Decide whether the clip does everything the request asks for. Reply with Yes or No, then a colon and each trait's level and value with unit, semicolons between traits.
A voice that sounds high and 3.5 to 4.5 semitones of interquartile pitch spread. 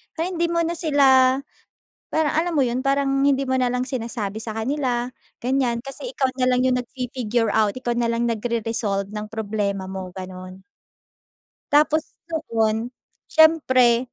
Yes: high, 245 Hz; average, 3.9 semitones